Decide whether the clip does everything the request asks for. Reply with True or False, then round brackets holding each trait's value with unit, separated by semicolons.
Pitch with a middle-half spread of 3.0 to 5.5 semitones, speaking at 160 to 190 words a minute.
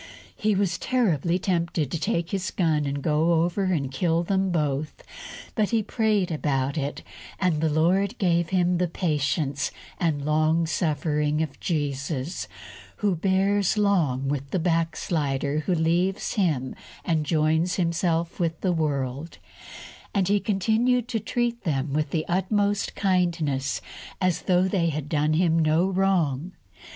False (3.9 semitones; 145 wpm)